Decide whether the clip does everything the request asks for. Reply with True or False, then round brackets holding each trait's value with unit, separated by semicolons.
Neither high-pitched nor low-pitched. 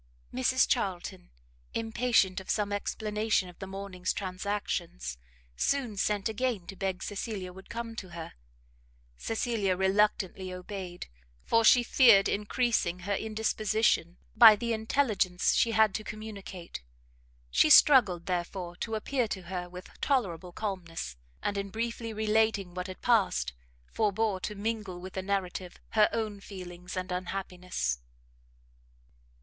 False (200 Hz)